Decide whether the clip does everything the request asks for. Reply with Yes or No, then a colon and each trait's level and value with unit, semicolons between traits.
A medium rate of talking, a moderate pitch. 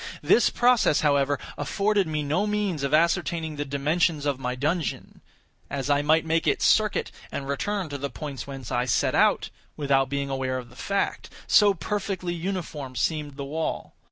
Yes: average, 175 wpm; medium, 150 Hz